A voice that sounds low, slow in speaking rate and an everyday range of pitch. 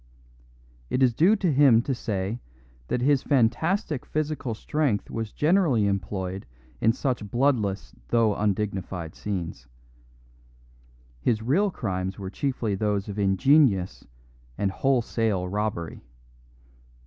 No: low, 110 Hz; slow, 110 wpm; wide, 5.7 semitones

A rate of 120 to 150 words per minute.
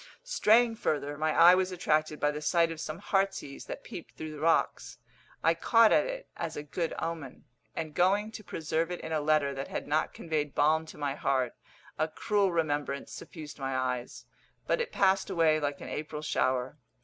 No: average, 195 wpm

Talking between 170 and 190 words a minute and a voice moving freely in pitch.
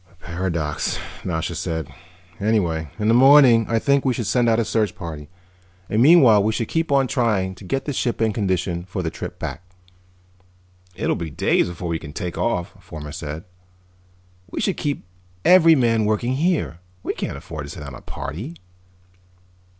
Yes: average, 180 wpm; wide, 6.7 semitones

